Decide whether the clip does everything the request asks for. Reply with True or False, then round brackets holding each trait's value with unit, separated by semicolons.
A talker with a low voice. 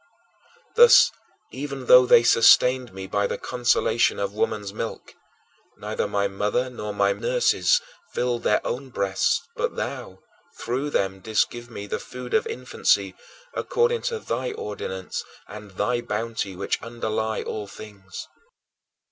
True (115 Hz)